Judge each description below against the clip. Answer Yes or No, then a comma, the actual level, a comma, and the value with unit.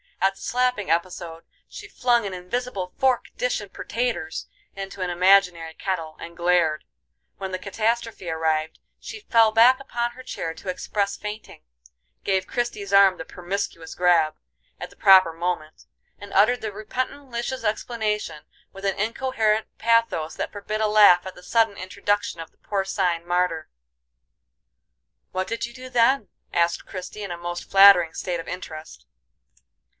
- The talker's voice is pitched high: Yes, high, 195 Hz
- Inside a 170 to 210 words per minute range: No, average, 155 wpm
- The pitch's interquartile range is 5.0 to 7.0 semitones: No, average, 4.4 semitones